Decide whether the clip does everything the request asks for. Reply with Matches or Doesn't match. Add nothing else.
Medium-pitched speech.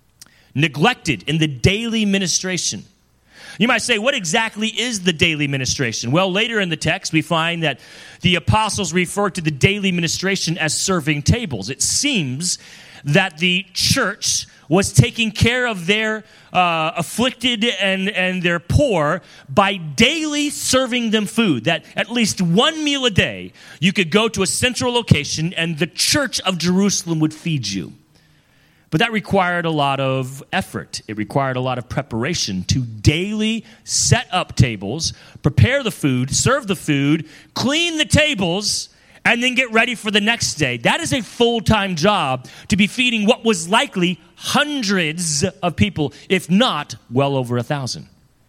Matches